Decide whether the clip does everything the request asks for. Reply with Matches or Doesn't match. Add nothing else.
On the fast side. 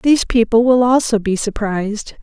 Doesn't match